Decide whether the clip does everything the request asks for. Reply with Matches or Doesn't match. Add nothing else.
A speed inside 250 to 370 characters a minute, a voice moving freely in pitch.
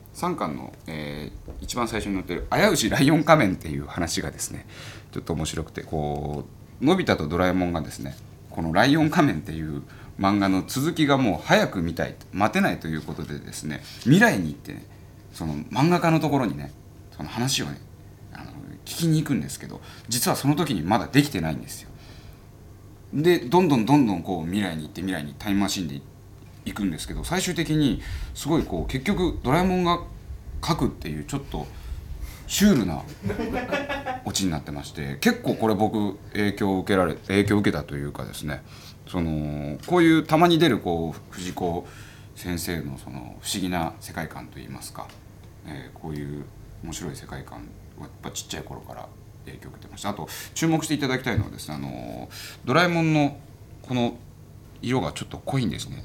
Doesn't match